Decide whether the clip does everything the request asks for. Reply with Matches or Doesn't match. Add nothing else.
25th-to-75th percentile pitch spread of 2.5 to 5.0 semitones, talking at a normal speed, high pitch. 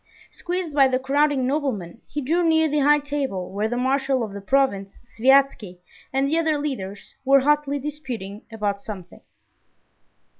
Doesn't match